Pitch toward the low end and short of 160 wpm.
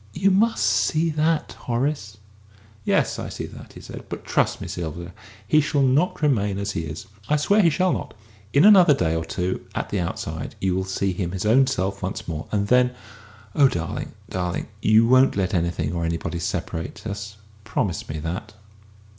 No: low, 100 Hz; average, 190 wpm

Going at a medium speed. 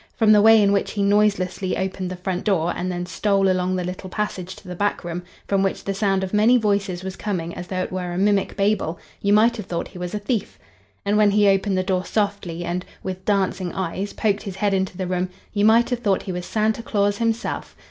No: fast, 240 wpm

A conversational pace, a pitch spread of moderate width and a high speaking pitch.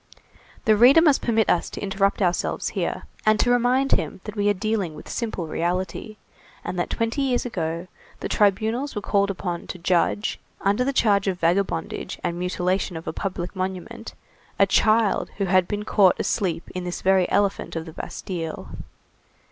Yes: average, 175 wpm; average, 3.5 semitones; high, 195 Hz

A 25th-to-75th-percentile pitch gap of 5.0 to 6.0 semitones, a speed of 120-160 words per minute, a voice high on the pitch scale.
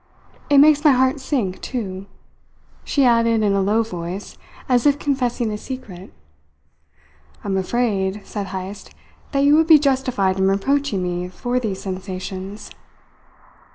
Yes: wide, 5.6 semitones; average, 140 wpm; high, 215 Hz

